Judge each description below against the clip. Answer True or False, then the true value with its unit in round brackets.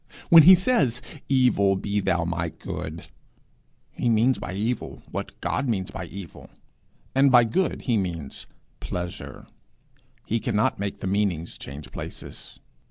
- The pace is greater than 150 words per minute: False (140 wpm)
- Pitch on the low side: True (100 Hz)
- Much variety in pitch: True (5.9 semitones)